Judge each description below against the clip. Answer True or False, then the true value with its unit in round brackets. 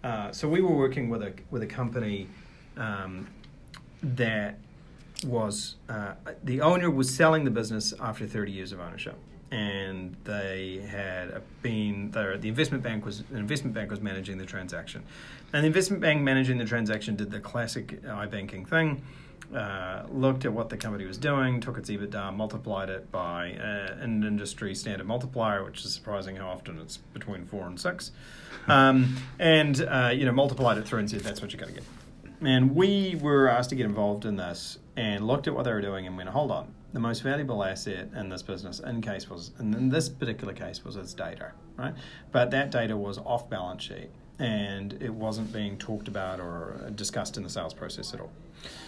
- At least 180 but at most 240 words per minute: True (195 wpm)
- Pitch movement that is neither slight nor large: True (4.6 semitones)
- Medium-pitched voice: False (110 Hz)